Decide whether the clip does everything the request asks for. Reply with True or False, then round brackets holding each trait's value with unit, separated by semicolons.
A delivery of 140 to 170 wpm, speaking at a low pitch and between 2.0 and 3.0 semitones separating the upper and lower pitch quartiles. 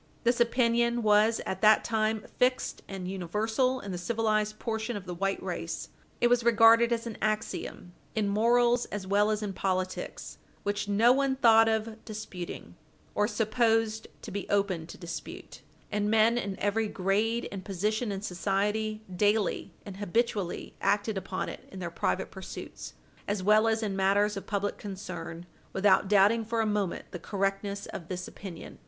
False (165 wpm; 210 Hz; 2.5 semitones)